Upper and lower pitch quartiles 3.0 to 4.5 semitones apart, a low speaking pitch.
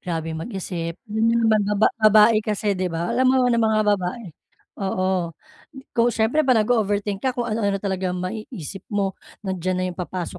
No: average, 3.4 semitones; high, 205 Hz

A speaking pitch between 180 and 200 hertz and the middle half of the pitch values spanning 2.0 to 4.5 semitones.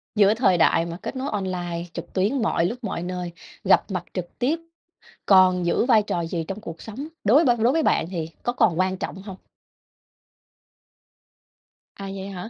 Yes: high, 190 Hz; average, 4.2 semitones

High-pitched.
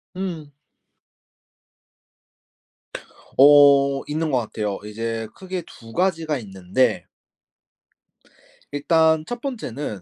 No: medium, 145 Hz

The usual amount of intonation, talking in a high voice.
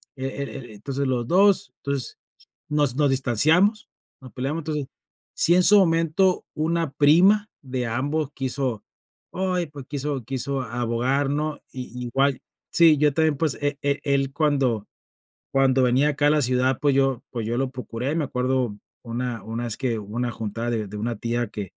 No: average, 3.5 semitones; low, 135 Hz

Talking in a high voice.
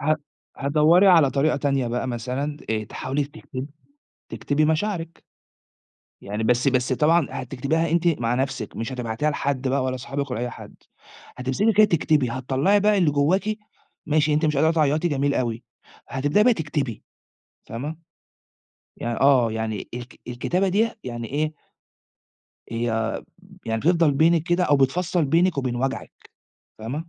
No: medium, 140 Hz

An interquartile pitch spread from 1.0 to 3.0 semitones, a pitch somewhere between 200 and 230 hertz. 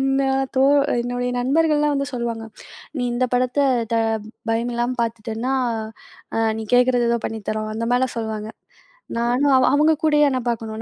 No: average, 2.7 semitones; high, 245 Hz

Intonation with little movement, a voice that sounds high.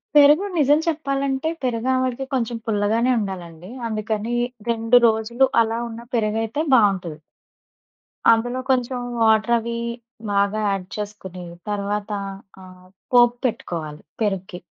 No: average, 3.4 semitones; high, 225 Hz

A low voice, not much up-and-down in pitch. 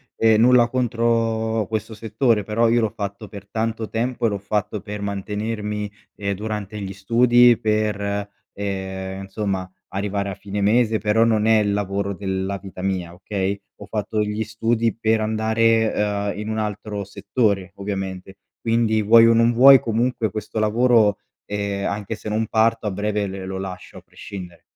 Yes: low, 105 Hz; narrow, 2.1 semitones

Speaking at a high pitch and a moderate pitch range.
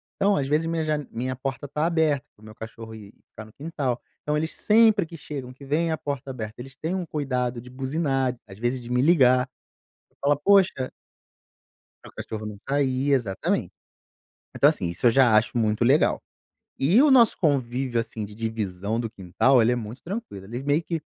No: low, 130 Hz; average, 4.8 semitones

